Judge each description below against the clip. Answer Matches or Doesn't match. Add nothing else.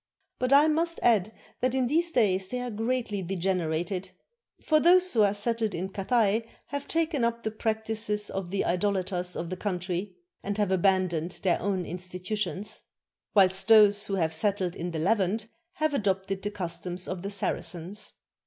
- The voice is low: Doesn't match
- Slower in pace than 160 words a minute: Doesn't match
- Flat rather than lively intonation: Doesn't match